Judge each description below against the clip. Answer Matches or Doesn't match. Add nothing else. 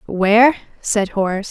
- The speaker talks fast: Doesn't match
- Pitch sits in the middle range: Doesn't match